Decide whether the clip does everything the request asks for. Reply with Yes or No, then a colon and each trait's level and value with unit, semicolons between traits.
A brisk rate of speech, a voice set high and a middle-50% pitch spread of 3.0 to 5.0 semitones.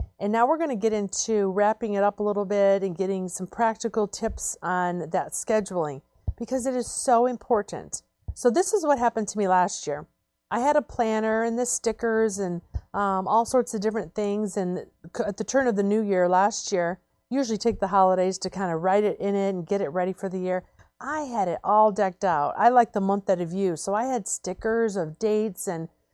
Yes: fast, 225 wpm; high, 205 Hz; average, 3.3 semitones